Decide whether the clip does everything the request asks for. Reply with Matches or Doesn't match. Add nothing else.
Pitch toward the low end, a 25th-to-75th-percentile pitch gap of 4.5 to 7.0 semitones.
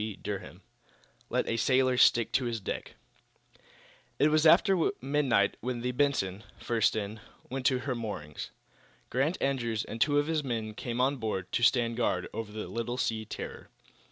Doesn't match